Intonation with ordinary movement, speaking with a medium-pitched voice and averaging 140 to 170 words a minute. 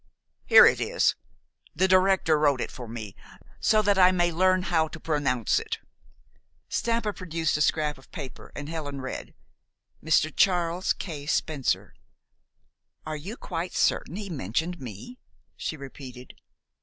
Yes: average, 4.7 semitones; medium, 160 Hz; average, 145 wpm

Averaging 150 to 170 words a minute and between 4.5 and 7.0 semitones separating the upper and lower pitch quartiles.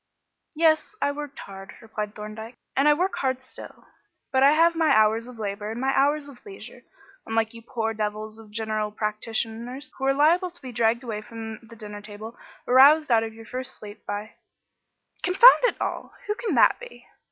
No: average, 195 wpm; average, 4.8 semitones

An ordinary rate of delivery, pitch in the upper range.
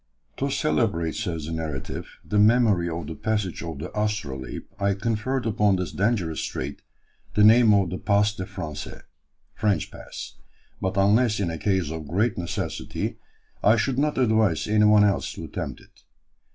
No: average, 165 wpm; low, 100 Hz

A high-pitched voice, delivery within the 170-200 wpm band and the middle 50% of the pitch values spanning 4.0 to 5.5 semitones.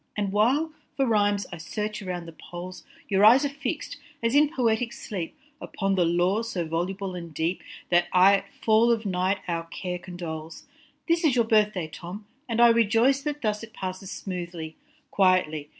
Yes: high, 195 Hz; average, 185 wpm; average, 4.5 semitones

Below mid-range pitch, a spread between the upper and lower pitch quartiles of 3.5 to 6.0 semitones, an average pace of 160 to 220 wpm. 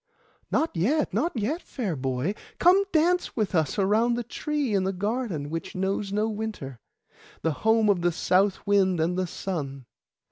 No: high, 200 Hz; average, 5.3 semitones; average, 170 wpm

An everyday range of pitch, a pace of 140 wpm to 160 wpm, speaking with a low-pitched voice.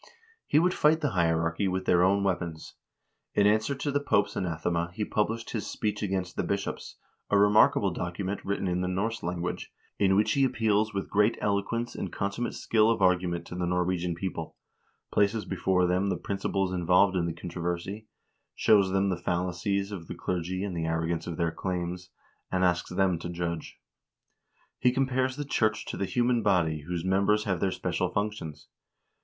No: average, 3.1 semitones; average, 185 wpm; very low, 95 Hz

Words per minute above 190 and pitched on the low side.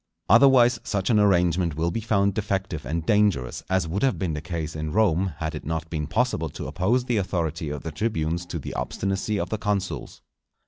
Yes: average, 200 wpm; very low, 90 Hz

